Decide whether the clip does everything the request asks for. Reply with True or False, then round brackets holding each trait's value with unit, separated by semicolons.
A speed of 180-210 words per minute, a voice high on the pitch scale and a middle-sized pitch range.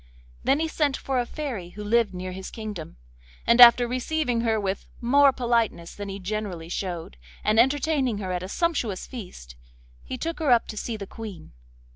True (185 wpm; 225 Hz; 5.0 semitones)